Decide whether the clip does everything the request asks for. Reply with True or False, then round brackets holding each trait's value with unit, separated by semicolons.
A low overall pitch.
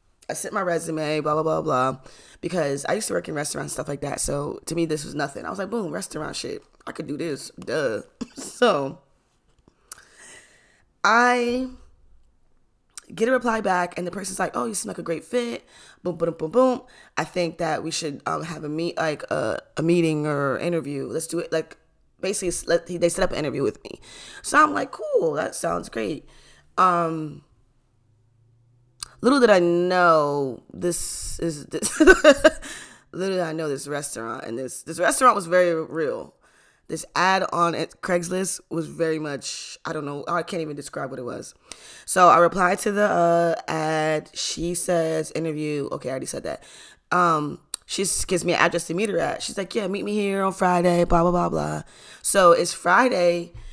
False (170 Hz)